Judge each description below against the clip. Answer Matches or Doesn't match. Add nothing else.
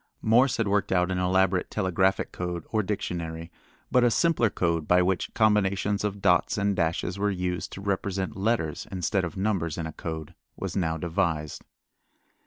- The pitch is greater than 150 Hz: Doesn't match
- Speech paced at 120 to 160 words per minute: Doesn't match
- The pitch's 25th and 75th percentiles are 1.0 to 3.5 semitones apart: Matches